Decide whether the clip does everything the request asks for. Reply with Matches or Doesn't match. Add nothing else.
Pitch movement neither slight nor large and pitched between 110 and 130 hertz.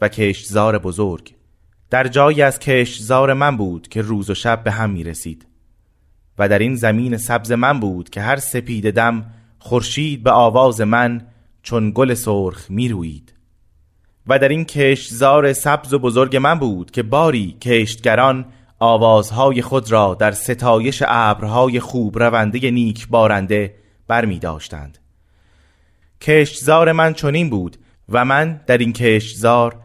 Matches